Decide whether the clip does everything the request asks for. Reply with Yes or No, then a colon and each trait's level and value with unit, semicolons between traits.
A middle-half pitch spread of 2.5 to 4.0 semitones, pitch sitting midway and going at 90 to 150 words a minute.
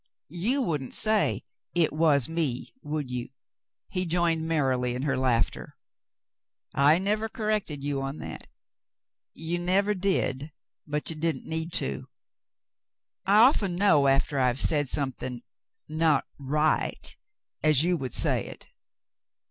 No: average, 4.4 semitones; medium, 155 Hz; average, 140 wpm